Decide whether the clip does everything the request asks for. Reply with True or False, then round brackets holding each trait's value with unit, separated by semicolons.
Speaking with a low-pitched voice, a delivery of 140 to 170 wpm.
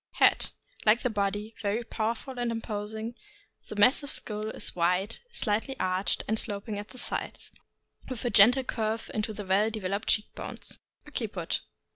False (215 Hz; 160 wpm)